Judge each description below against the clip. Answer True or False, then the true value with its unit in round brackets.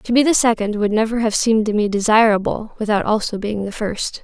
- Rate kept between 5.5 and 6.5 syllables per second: True (5.8 syllables/s)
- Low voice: False (215 Hz)